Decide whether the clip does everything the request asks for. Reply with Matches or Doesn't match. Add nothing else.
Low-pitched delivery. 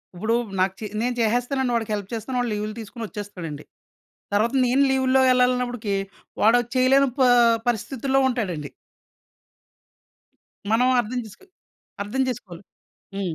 Doesn't match